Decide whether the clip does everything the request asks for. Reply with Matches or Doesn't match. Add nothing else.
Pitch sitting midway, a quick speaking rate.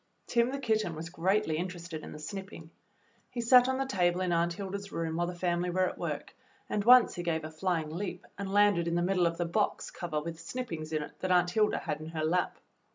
Matches